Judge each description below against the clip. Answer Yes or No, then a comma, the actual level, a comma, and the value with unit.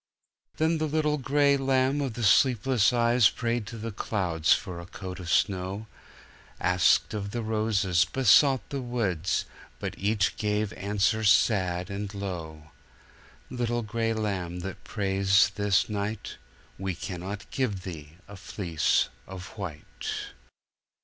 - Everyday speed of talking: No, slow, 130 wpm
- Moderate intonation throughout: Yes, average, 4.1 semitones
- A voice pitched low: Yes, low, 105 Hz